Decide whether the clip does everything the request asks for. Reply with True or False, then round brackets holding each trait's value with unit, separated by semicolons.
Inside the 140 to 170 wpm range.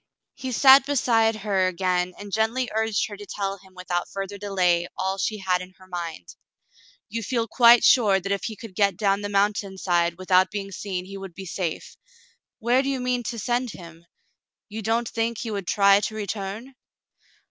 False (190 wpm)